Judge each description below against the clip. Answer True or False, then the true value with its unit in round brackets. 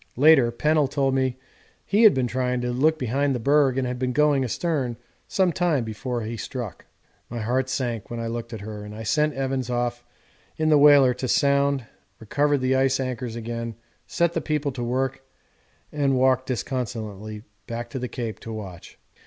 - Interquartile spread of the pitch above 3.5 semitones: False (3.1 semitones)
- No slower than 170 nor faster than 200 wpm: True (185 wpm)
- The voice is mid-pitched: False (130 Hz)